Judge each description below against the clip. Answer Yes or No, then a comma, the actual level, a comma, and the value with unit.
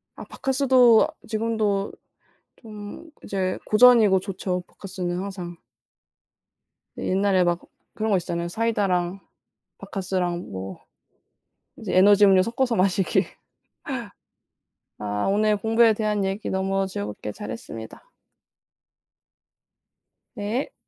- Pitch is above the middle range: Yes, high, 195 Hz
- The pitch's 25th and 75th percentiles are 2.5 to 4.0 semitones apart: Yes, average, 3.2 semitones